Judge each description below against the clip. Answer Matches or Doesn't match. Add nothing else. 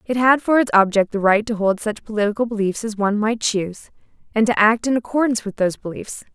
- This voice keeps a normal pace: Doesn't match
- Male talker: Doesn't match